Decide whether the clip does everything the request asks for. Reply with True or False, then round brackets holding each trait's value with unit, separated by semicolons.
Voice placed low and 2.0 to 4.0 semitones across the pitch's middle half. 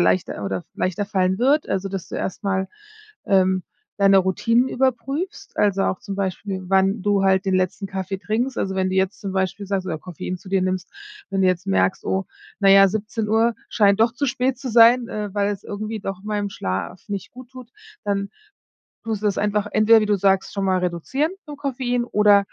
False (200 Hz; 2.7 semitones)